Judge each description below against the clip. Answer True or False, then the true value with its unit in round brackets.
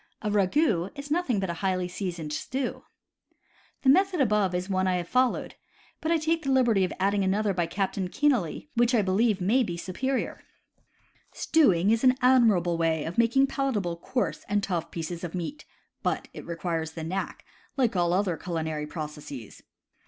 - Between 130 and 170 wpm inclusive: False (180 wpm)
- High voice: True (195 Hz)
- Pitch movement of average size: False (6.6 semitones)